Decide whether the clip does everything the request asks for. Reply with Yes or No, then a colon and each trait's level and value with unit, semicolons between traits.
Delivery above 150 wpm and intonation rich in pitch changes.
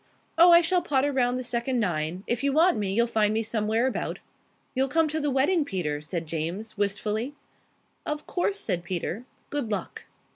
Yes: average, 185 wpm; wide, 6.3 semitones